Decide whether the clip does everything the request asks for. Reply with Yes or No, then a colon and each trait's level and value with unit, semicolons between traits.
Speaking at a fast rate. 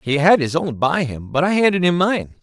Yes: fast, 270 wpm